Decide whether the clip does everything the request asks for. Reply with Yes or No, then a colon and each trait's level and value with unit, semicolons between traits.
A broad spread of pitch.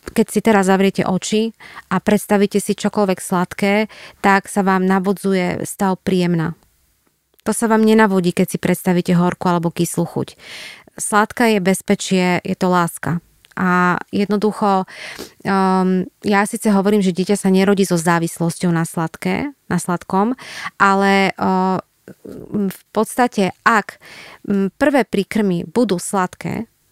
No: narrow, 2.5 semitones